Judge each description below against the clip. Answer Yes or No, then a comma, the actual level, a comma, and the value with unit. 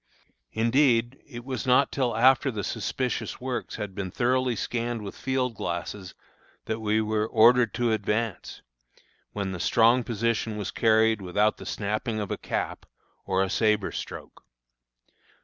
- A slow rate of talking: No, average, 150 wpm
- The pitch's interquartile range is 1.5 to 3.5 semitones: Yes, average, 2.7 semitones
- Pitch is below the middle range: Yes, low, 110 Hz